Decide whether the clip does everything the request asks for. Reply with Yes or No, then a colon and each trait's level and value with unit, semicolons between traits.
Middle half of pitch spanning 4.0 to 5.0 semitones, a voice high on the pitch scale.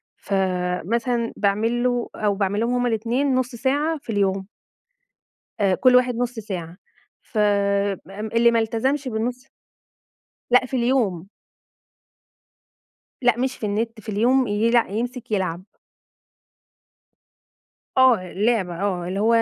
No: average, 3.6 semitones; high, 225 Hz